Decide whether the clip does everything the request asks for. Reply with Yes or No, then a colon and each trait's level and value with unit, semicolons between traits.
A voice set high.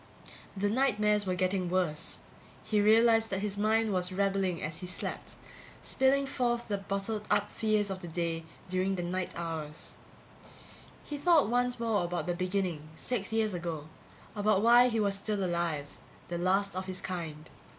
Yes: high, 195 Hz